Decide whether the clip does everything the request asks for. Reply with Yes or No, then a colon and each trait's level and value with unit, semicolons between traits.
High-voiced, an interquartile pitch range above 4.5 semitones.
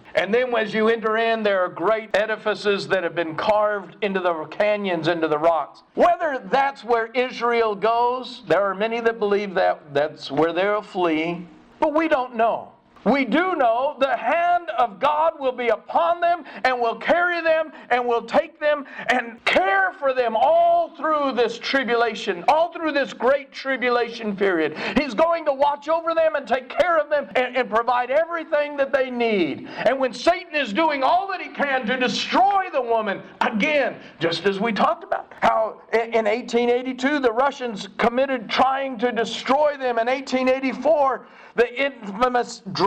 Yes: high, 245 Hz; average, 5.0 semitones